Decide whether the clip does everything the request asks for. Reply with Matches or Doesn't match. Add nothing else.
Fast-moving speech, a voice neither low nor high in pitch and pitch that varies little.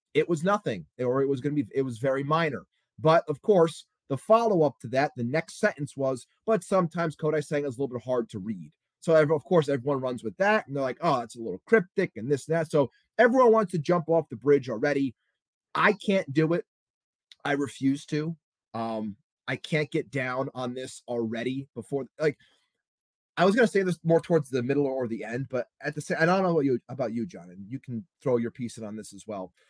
Doesn't match